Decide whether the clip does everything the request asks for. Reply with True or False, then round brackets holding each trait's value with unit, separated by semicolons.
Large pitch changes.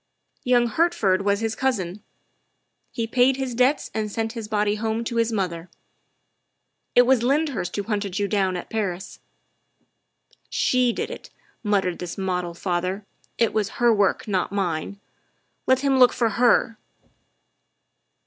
False (3.9 semitones)